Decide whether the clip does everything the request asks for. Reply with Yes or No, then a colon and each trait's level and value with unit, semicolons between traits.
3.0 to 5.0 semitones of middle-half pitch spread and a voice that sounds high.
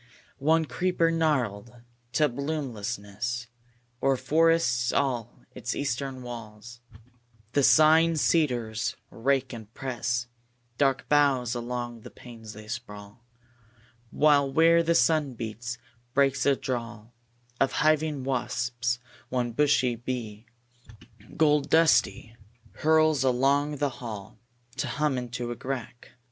No: average, 3.6 semitones; low, 130 Hz